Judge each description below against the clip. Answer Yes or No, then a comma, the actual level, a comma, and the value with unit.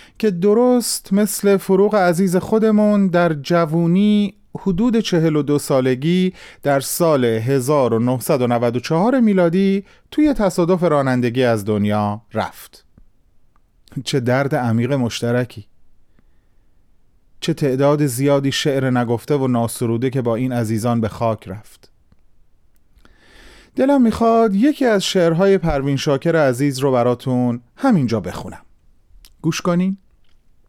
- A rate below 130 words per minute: Yes, slow, 105 wpm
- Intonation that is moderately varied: No, wide, 8.1 semitones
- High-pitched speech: No, medium, 140 Hz